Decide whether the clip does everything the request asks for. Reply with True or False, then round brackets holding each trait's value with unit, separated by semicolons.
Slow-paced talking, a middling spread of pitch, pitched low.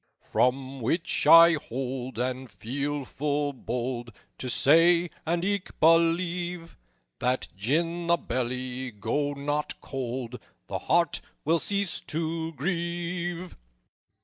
False (110 wpm; 4.8 semitones; 145 Hz)